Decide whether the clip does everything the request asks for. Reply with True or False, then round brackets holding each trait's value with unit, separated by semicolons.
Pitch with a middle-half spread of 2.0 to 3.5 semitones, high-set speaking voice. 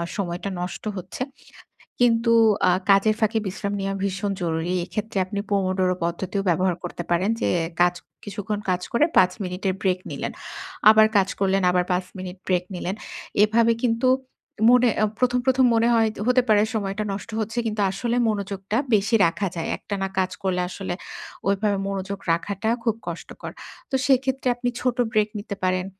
True (3.1 semitones; 200 Hz)